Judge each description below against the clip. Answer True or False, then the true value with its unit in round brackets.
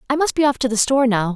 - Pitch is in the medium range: False (250 Hz)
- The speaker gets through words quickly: True (355 wpm)